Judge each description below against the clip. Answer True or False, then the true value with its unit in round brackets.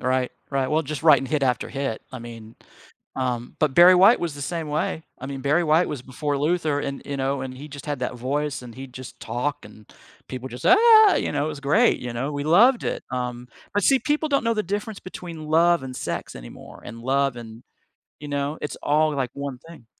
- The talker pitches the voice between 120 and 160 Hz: True (140 Hz)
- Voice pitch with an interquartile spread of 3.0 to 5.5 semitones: True (4.1 semitones)